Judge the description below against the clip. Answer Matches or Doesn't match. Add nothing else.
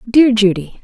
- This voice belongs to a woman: Matches